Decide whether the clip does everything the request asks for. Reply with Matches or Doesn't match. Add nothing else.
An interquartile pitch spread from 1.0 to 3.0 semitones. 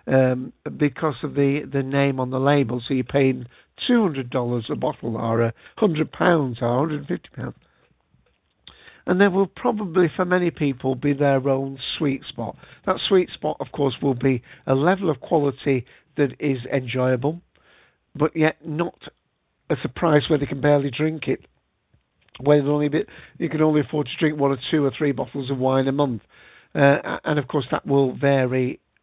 Matches